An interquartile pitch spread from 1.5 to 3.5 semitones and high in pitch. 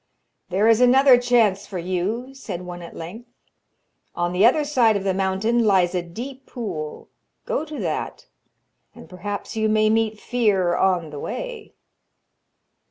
No: average, 5.0 semitones; high, 210 Hz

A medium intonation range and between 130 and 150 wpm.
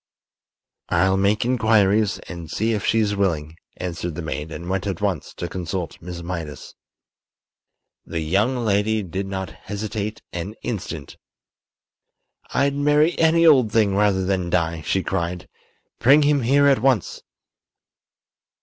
Yes: average, 4.5 semitones; slow, 135 wpm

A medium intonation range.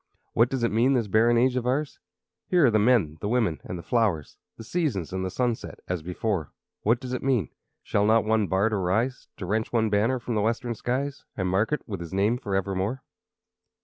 Yes: average, 4.2 semitones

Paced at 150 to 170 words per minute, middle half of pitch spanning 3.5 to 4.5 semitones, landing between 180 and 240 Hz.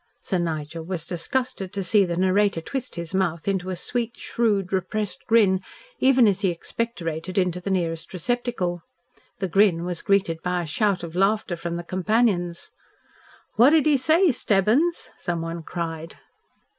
Yes: average, 155 wpm; average, 4.1 semitones; medium, 185 Hz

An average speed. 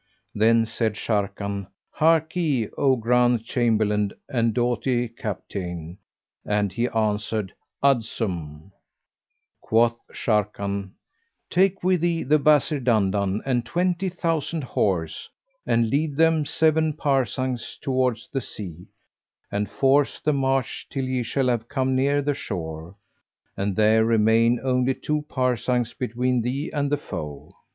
No: slow, 125 wpm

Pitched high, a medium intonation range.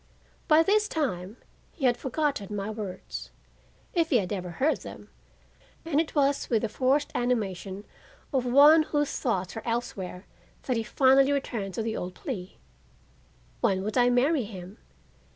No: high, 240 Hz; wide, 6.1 semitones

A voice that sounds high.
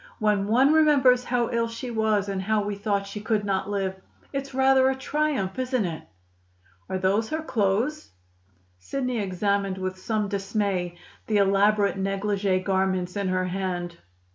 Yes: high, 205 Hz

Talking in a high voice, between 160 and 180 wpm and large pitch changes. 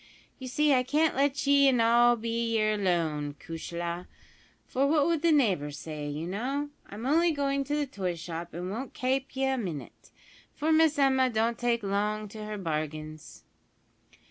Yes: high, 230 Hz; average, 175 wpm; wide, 7.8 semitones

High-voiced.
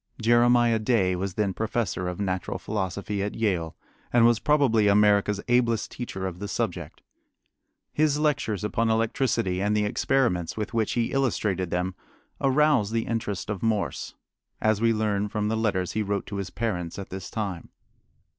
No: low, 105 Hz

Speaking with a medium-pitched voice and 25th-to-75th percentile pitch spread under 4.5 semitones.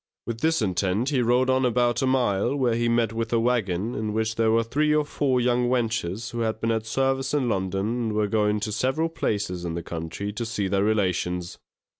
No: low, 115 Hz; average, 3.3 semitones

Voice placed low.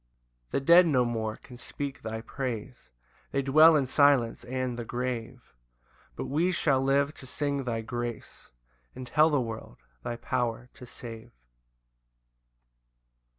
Yes: low, 125 Hz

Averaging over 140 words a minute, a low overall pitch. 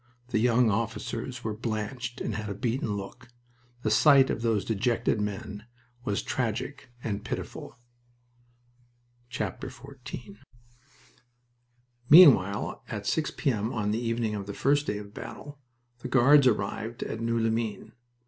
No: slow, 135 wpm; low, 115 Hz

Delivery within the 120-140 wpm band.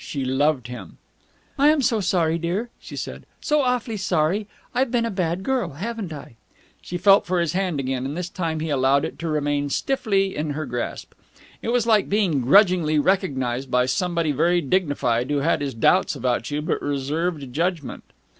No: average, 185 wpm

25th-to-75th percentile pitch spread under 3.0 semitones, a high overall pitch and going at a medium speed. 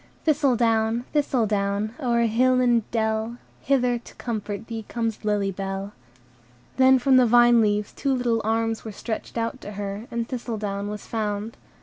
Yes: narrow, 2.5 semitones; high, 225 Hz; average, 150 wpm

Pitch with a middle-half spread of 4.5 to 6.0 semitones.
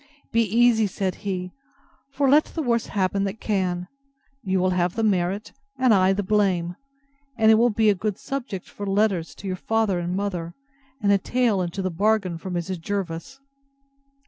No: average, 3.3 semitones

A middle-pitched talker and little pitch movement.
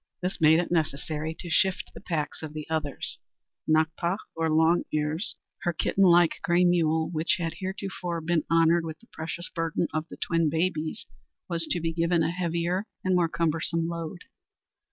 Yes: medium, 165 Hz; narrow, 1.5 semitones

